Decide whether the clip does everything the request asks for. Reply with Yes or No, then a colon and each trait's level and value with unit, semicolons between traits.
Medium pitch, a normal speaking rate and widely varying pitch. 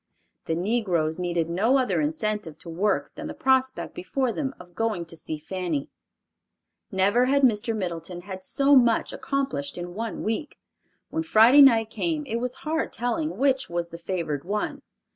No: high, 215 Hz; average, 165 wpm; wide, 7.0 semitones